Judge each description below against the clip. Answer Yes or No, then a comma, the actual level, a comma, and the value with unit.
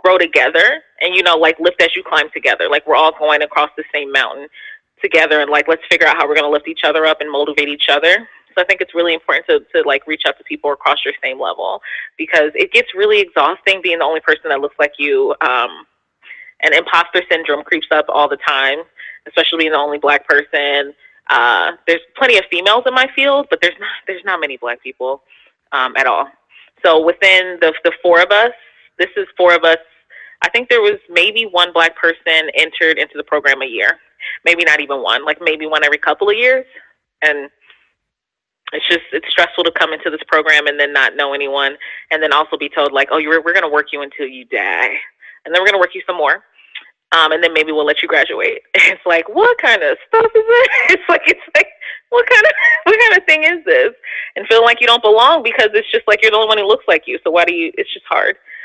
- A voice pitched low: No, medium, 170 Hz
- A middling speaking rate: No, fast, 235 wpm